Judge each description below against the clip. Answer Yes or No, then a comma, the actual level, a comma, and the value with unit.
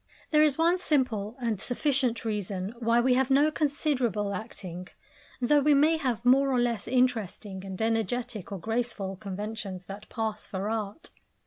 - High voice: Yes, high, 230 Hz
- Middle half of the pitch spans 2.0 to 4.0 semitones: No, average, 4.5 semitones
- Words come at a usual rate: Yes, average, 155 wpm